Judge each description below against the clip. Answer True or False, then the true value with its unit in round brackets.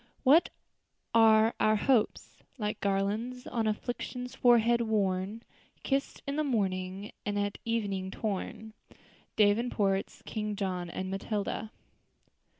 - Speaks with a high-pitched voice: True (215 Hz)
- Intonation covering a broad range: False (3.0 semitones)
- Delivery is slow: True (110 wpm)